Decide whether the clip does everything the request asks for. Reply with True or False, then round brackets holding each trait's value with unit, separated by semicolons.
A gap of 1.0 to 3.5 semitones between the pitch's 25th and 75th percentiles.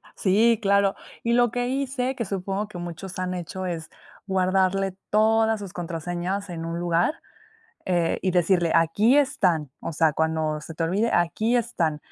False (4.1 semitones)